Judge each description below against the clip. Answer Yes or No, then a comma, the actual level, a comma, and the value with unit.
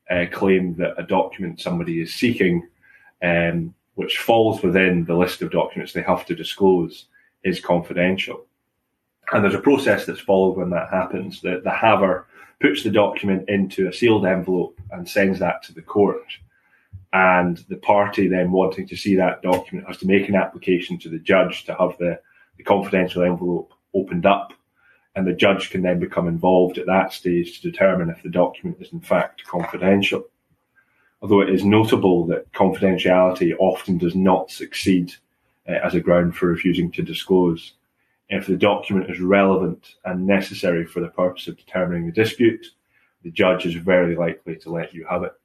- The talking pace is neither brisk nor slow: Yes, average, 175 wpm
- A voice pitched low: Yes, very low, 90 Hz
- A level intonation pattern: Yes, narrow, 1.8 semitones